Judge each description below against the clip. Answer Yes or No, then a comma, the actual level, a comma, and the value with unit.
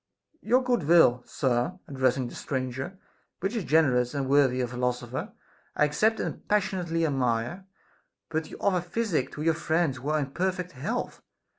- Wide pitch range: Yes, wide, 5.8 semitones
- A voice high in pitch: No, medium, 150 Hz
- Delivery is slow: No, average, 160 wpm